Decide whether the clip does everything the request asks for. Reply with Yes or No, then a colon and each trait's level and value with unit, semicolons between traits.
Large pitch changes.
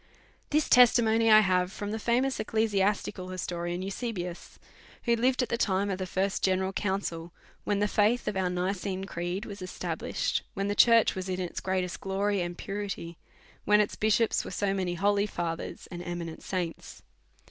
No: narrow, 2.5 semitones